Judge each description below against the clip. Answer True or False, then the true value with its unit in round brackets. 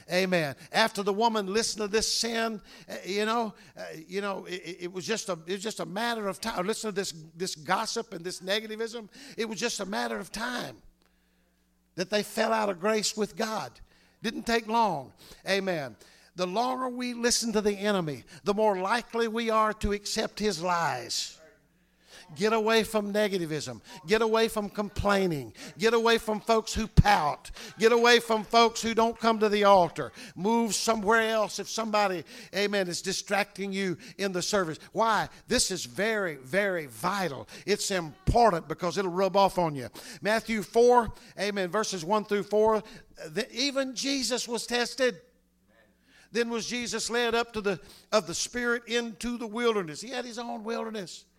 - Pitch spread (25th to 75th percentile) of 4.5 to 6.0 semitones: False (3.5 semitones)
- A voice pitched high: True (210 Hz)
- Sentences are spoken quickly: False (175 wpm)